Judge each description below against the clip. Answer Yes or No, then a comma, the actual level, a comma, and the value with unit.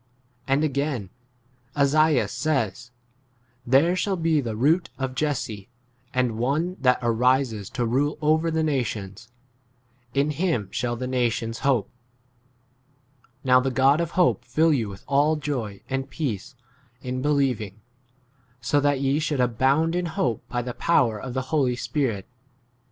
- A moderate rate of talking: Yes, average, 145 wpm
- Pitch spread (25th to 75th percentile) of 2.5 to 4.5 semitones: Yes, average, 3.9 semitones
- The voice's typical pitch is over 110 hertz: Yes, low, 135 Hz